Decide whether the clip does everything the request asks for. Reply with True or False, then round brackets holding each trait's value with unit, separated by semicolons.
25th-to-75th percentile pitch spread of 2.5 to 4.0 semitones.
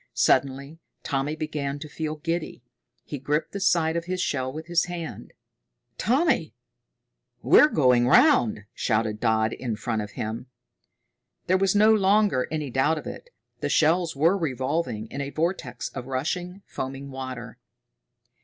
False (5.0 semitones)